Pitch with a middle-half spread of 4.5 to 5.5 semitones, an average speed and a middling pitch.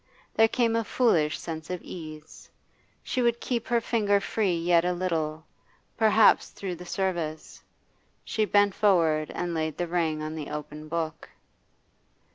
Yes: average, 4.8 semitones; average, 150 wpm; medium, 175 Hz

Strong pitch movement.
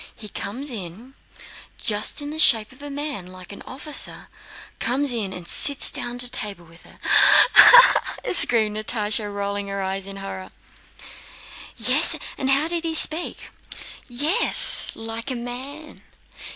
Yes: wide, 5.9 semitones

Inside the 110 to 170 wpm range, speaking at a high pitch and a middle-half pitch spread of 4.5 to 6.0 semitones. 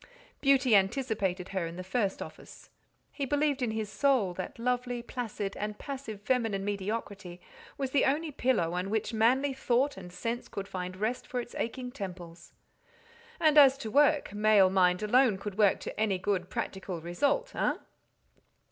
Yes: average, 160 wpm; high, 215 Hz; average, 5.2 semitones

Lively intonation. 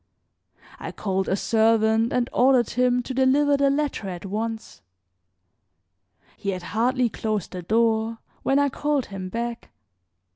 No: average, 3.5 semitones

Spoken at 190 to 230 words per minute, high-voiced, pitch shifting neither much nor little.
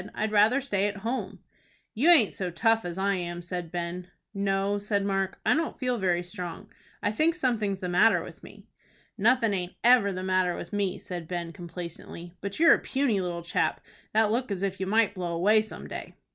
Yes: average, 200 wpm; high, 200 Hz; average, 3.7 semitones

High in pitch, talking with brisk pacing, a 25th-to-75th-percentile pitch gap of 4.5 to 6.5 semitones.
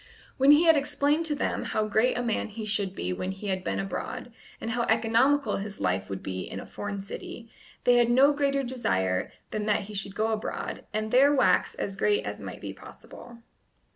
Yes: high, 220 Hz; fast, 210 wpm; average, 4.8 semitones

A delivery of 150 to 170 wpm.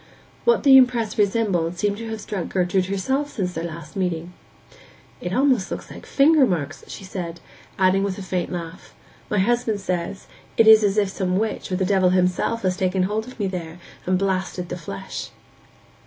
No: average, 185 wpm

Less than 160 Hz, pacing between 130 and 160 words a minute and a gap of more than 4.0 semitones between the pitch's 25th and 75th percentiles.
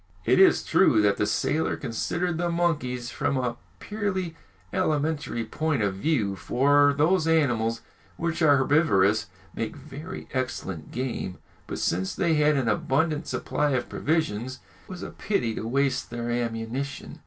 Yes: medium, 140 Hz; average, 150 wpm; wide, 5.6 semitones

